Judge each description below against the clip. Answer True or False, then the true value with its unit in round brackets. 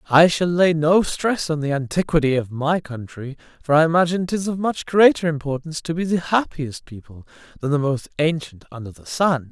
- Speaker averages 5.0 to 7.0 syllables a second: True (5.4 syllables/s)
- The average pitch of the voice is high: False (155 Hz)